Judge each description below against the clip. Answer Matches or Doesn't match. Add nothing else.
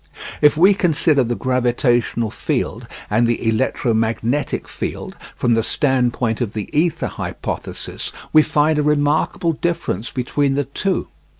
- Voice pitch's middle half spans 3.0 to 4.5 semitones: Matches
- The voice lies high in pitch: Doesn't match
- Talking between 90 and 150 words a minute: Matches